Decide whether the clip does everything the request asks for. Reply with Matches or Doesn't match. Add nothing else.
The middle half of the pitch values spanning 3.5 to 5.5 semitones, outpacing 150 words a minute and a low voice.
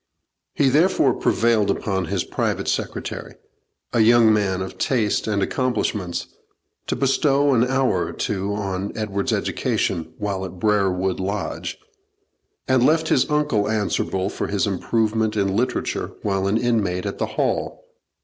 Doesn't match